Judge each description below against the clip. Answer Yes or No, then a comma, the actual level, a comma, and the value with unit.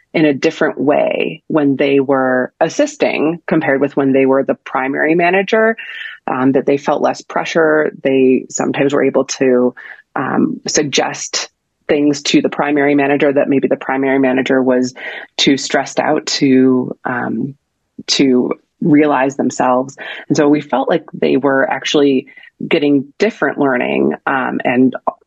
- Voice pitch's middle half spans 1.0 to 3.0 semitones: Yes, narrow, 2.4 semitones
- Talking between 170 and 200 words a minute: No, average, 145 wpm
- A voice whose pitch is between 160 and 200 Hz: No, medium, 140 Hz